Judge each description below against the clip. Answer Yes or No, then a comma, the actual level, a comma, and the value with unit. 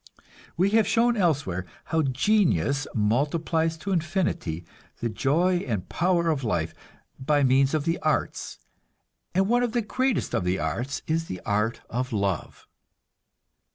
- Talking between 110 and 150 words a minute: Yes, average, 145 wpm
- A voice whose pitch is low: No, medium, 145 Hz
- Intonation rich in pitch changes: Yes, wide, 7.6 semitones